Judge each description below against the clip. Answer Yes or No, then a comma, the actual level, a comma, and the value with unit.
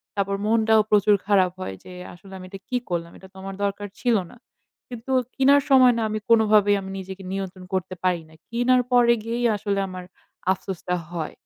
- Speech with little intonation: No, average, 3.6 semitones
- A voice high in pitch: Yes, high, 200 Hz